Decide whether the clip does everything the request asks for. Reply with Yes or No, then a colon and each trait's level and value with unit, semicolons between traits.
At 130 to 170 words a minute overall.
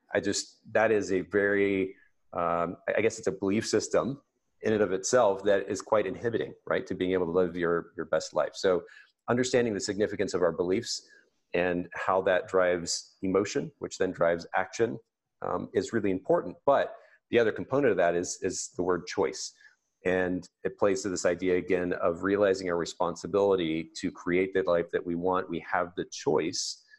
No: average, 185 wpm